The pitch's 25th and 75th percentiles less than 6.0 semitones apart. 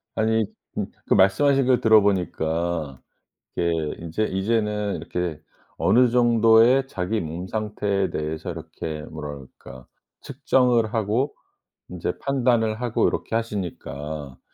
Yes: wide, 5.6 semitones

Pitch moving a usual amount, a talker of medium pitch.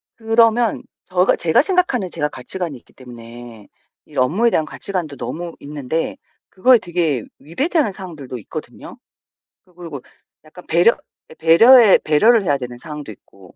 No: wide, 7.3 semitones; medium, 170 Hz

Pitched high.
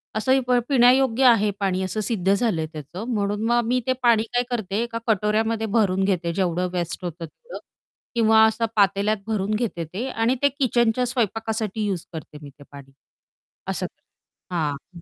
Yes: high, 215 Hz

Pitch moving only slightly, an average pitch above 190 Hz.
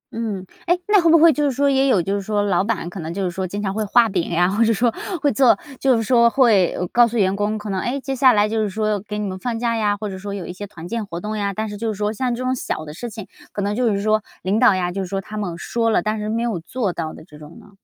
No: average, 3.3 semitones; high, 210 Hz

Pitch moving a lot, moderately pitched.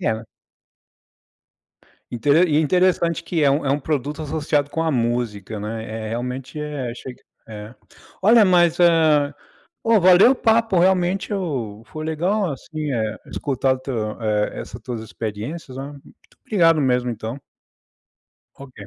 Yes: wide, 6.1 semitones; medium, 145 Hz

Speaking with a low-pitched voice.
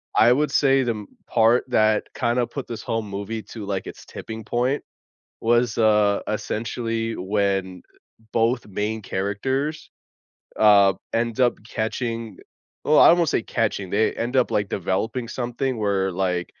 Yes: low, 110 Hz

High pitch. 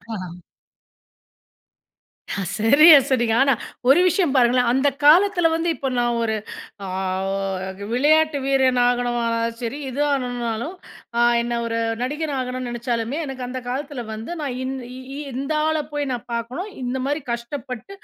Yes: very high, 255 Hz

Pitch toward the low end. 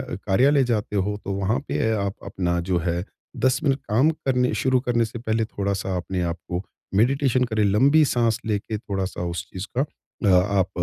Yes: low, 105 Hz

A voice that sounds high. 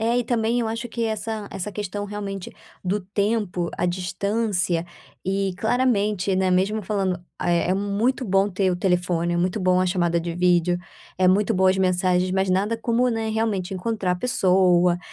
Yes: high, 195 Hz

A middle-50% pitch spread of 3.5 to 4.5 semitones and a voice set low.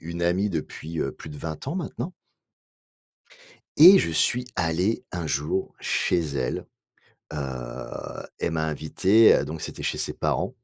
Yes: average, 4.0 semitones; very low, 80 Hz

